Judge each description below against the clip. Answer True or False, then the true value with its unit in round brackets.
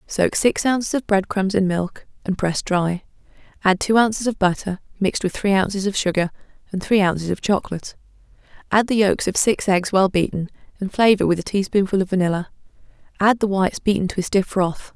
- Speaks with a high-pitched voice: True (195 Hz)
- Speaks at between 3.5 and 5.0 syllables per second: False (5.8 syllables/s)